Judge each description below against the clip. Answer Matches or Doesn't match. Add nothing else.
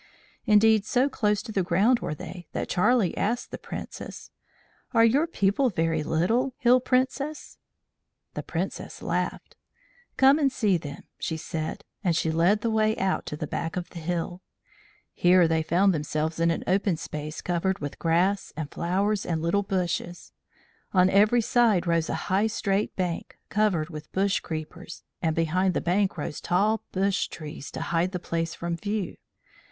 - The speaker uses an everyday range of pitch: Matches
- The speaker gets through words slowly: Doesn't match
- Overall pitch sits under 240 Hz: Matches